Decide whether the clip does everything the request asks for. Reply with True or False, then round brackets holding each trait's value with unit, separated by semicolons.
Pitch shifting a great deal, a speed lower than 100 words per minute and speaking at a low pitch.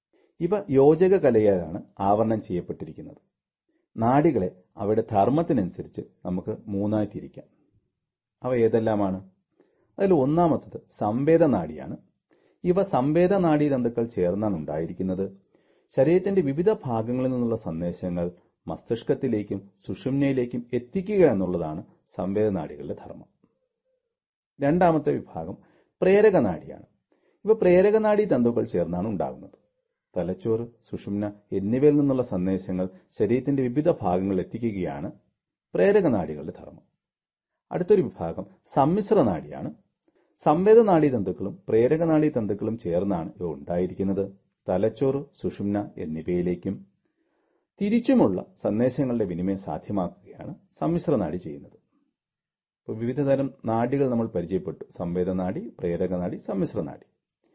True (7.7 semitones; 90 wpm; 115 Hz)